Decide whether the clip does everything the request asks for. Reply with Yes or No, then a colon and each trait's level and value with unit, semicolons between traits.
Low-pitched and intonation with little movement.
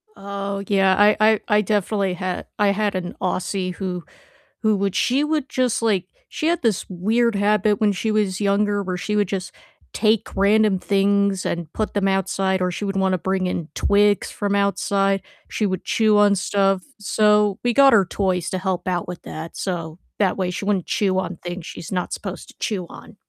No: high, 200 Hz; narrow, 2.0 semitones